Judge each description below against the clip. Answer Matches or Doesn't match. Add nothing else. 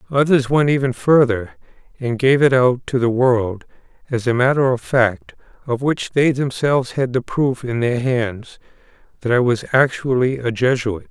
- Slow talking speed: Doesn't match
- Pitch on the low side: Matches